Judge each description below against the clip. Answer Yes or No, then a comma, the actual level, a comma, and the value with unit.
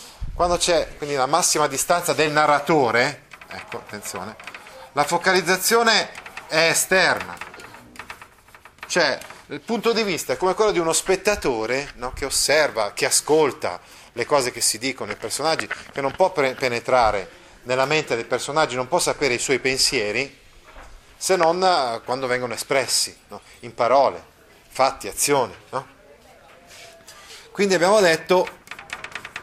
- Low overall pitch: No, medium, 155 Hz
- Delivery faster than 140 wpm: No, average, 135 wpm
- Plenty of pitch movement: Yes, wide, 5.7 semitones